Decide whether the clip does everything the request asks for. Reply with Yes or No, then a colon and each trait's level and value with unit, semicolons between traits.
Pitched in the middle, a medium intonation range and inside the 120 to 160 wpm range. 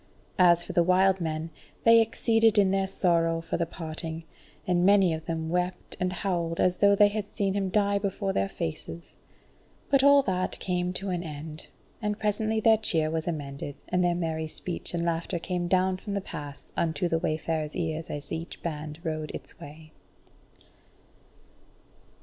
No: medium, 175 Hz; average, 3.4 semitones; average, 175 wpm